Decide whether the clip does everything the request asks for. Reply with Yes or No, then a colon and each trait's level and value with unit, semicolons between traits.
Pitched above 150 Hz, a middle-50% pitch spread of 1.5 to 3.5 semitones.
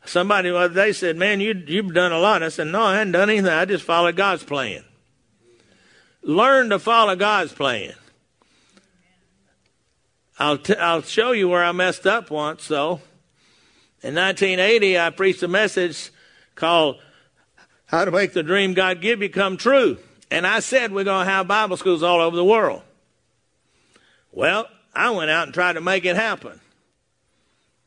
Yes: medium, 185 Hz; average, 2.7 semitones